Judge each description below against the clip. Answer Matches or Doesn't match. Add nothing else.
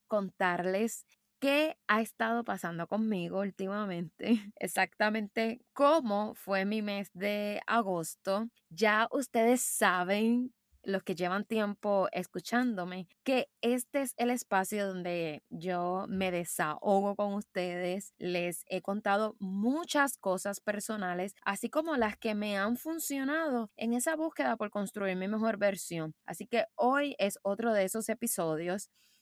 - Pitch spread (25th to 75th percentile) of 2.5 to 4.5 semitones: Matches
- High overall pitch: Matches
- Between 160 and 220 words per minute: Doesn't match